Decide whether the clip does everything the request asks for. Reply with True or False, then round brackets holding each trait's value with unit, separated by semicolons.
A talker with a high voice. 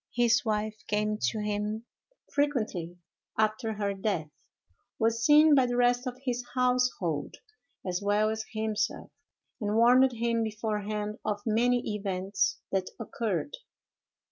True (220 Hz)